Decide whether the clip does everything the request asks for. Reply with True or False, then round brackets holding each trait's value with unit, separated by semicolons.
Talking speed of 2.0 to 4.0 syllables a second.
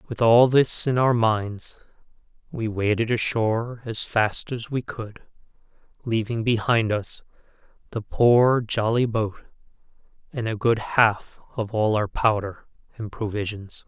True (3.9 syllables/s)